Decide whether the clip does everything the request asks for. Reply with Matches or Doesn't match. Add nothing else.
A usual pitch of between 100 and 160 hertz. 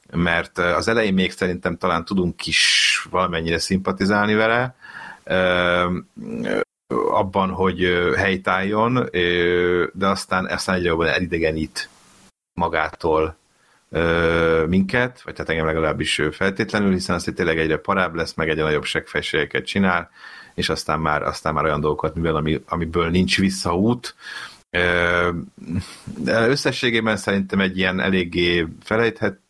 Doesn't match